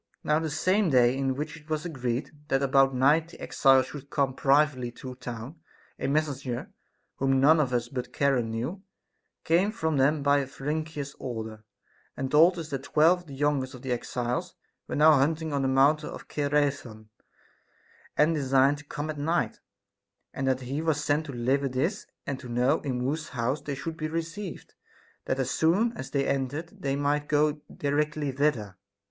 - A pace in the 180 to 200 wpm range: Yes, average, 185 wpm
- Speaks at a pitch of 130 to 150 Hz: Yes, medium, 140 Hz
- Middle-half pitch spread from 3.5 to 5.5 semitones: No, average, 2.8 semitones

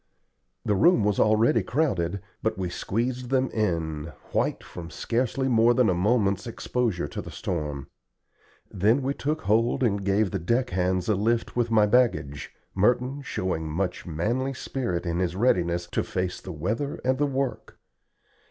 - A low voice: Yes, low, 105 Hz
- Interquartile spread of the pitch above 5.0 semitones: Yes, wide, 5.6 semitones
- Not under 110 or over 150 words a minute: No, average, 160 wpm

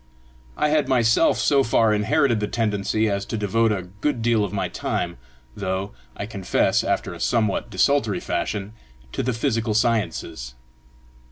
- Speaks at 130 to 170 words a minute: Yes, average, 155 wpm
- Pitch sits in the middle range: No, low, 110 Hz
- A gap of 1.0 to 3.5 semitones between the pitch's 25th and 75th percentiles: Yes, average, 2.8 semitones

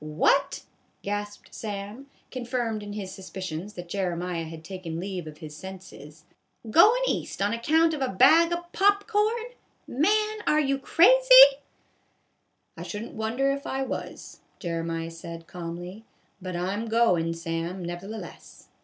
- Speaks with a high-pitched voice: Yes, high, 205 Hz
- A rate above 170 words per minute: No, average, 160 wpm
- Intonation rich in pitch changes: Yes, wide, 8.0 semitones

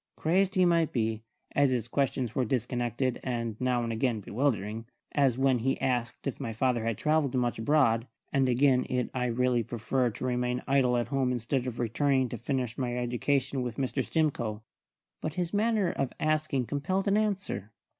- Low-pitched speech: Yes, low, 125 Hz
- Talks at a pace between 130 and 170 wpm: No, average, 180 wpm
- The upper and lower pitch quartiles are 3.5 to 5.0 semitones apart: No, average, 3.0 semitones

